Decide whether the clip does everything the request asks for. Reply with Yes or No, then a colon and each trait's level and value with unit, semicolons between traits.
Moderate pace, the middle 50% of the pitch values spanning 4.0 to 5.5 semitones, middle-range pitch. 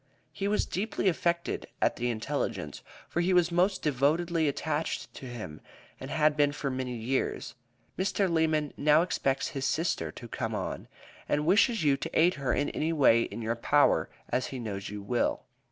Yes: average, 180 wpm; average, 5.2 semitones; medium, 150 Hz